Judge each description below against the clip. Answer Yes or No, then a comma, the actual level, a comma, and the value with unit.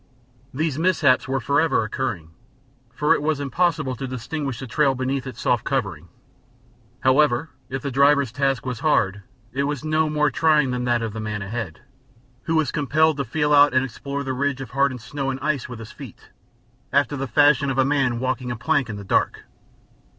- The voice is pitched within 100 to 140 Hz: Yes, low, 135 Hz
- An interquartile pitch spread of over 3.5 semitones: No, average, 2.9 semitones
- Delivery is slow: No, average, 195 wpm